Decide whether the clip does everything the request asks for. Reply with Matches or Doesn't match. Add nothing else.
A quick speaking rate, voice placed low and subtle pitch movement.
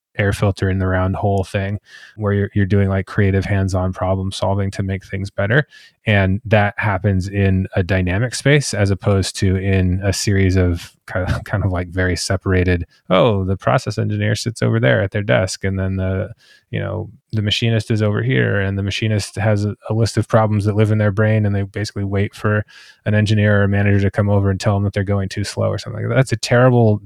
Matches